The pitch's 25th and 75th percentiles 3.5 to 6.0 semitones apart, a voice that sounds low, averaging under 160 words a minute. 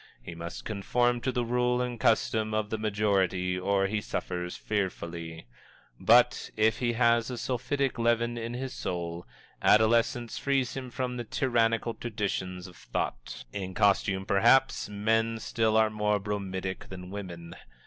Yes: average, 3.9 semitones; low, 110 Hz; average, 150 wpm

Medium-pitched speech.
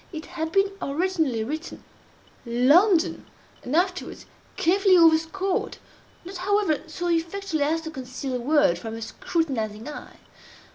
No: very high, 320 Hz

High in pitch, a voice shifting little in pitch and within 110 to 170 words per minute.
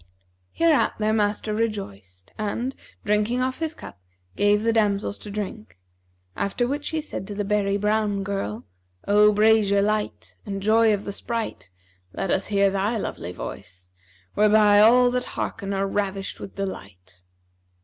Yes: high, 205 Hz; narrow, 1.9 semitones; average, 150 wpm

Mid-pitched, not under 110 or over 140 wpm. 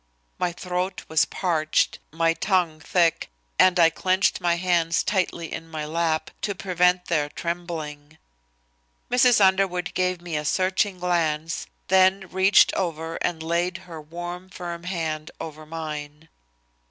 Yes: medium, 170 Hz; slow, 135 wpm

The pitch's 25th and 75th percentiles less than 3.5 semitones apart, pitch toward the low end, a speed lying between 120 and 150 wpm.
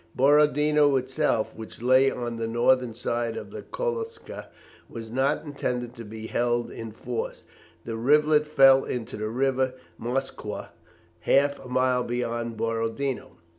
Yes: average, 3.1 semitones; low, 125 Hz; slow, 135 wpm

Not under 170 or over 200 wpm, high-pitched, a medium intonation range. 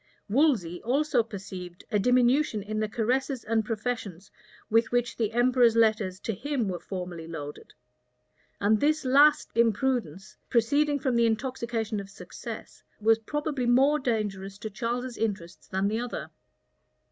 No: average, 145 wpm; high, 225 Hz; average, 3.8 semitones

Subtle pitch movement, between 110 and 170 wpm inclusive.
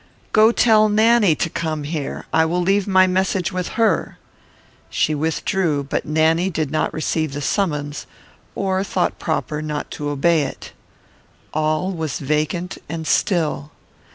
No: average, 3.7 semitones; average, 145 wpm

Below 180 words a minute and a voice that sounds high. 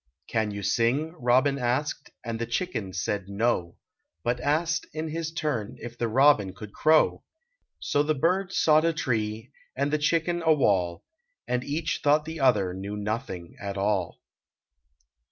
No: average, 160 wpm; low, 125 Hz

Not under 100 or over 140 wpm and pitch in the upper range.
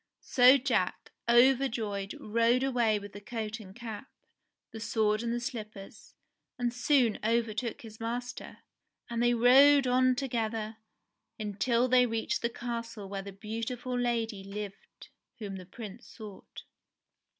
Yes: slow, 135 wpm; high, 230 Hz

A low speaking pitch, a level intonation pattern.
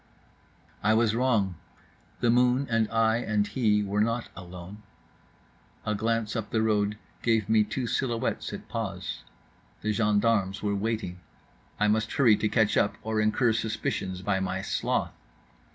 Yes: low, 110 Hz; narrow, 1.8 semitones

